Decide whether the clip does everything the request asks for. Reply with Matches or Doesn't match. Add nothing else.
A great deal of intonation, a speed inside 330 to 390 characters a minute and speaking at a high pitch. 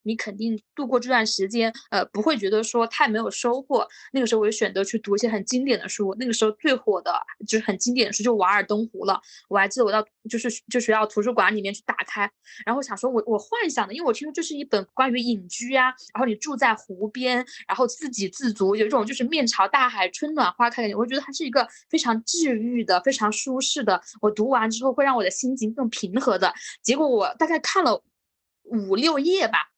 Doesn't match